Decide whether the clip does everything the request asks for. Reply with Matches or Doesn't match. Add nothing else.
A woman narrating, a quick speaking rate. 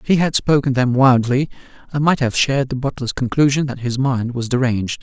Doesn't match